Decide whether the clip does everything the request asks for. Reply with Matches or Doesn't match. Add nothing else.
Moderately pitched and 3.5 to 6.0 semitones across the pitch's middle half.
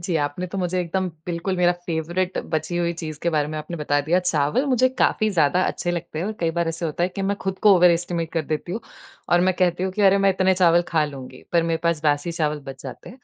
Doesn't match